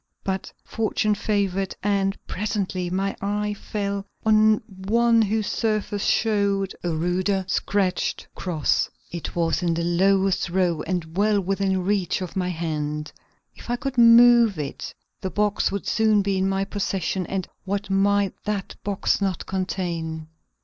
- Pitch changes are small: Yes, narrow, 2.3 semitones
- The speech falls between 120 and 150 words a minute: Yes, average, 145 wpm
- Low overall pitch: No, high, 195 Hz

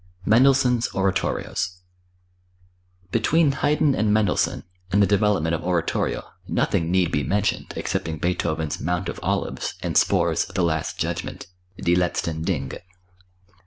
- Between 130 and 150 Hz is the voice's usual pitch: No, very low, 95 Hz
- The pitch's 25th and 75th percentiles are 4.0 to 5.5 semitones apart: Yes, average, 4.3 semitones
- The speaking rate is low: Yes, slow, 125 wpm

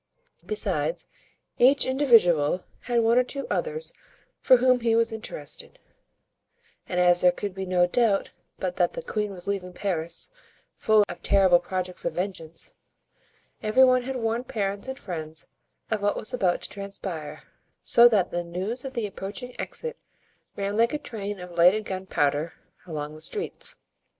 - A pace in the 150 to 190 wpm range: Yes, average, 160 wpm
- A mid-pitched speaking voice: No, high, 205 Hz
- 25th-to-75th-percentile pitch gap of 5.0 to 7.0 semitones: Yes, wide, 5.5 semitones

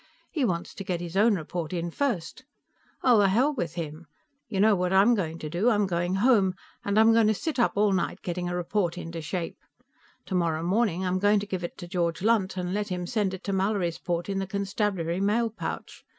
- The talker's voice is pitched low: No, high, 190 Hz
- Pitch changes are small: No, average, 3.2 semitones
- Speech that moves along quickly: Yes, fast, 220 wpm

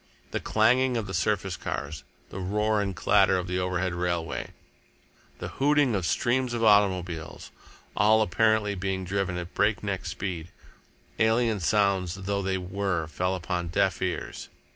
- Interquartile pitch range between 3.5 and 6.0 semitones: No, average, 2.9 semitones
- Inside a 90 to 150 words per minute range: Yes, average, 145 wpm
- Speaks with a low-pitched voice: Yes, very low, 95 Hz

